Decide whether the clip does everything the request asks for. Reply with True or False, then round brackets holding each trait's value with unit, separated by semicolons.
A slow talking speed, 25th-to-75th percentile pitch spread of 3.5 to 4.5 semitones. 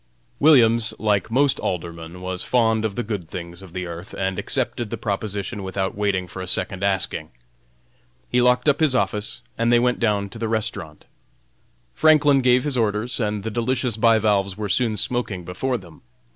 False (175 wpm; 4.1 semitones)